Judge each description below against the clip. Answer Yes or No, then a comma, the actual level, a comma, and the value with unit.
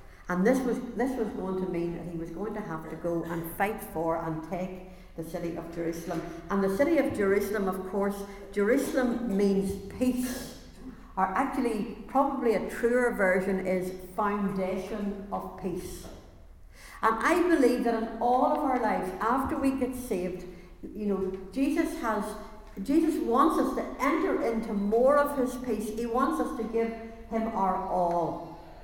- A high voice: Yes, high, 205 Hz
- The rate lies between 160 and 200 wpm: Yes, average, 165 wpm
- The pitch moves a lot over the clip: No, average, 4.8 semitones